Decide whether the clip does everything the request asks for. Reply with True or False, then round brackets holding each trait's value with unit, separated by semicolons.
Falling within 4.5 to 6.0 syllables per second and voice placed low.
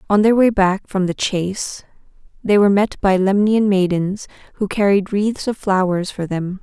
False (4.7 syllables/s; 195 Hz)